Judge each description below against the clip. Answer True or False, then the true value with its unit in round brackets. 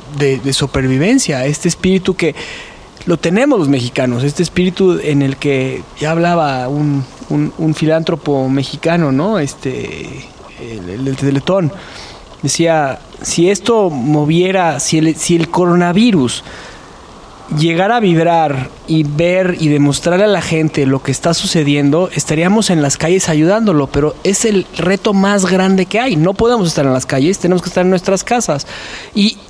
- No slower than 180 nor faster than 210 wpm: False (155 wpm)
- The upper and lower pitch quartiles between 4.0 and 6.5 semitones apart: True (4.5 semitones)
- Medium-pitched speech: True (160 Hz)